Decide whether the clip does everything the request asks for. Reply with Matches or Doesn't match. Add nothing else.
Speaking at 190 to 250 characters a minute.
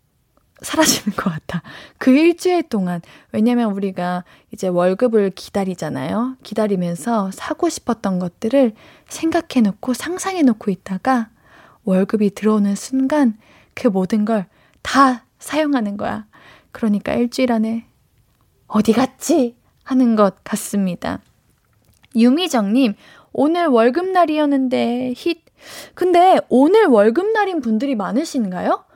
Doesn't match